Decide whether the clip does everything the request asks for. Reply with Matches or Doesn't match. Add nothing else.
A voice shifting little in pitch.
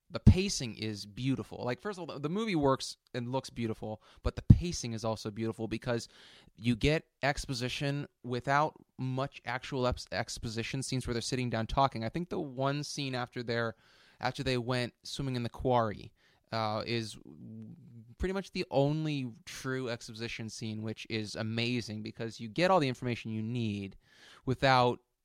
Doesn't match